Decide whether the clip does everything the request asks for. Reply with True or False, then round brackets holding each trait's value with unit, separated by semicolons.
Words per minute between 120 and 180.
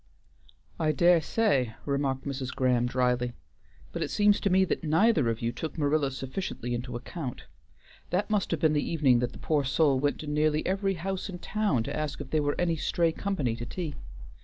False (200 wpm)